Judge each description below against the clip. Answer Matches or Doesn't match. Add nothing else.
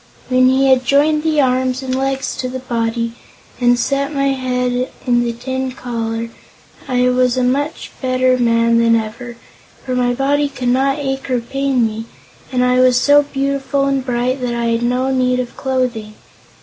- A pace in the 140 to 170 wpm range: Doesn't match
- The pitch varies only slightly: Matches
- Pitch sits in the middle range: Doesn't match